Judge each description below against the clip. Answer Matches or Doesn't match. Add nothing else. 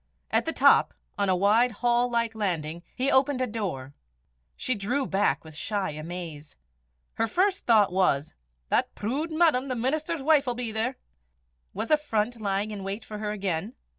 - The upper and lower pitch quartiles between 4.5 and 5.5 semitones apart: Matches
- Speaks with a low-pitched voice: Doesn't match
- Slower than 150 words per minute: Doesn't match